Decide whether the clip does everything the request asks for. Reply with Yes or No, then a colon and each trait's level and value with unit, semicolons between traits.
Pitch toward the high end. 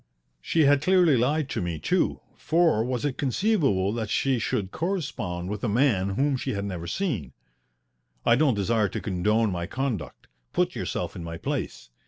No: low, 115 Hz